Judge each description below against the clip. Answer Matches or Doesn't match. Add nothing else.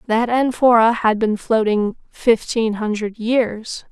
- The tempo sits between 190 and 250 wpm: Doesn't match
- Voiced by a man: Doesn't match